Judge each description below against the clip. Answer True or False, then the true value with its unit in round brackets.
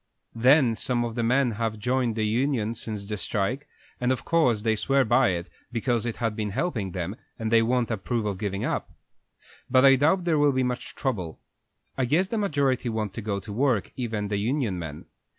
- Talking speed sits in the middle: False (210 wpm)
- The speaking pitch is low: True (115 Hz)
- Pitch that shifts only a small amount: False (3.7 semitones)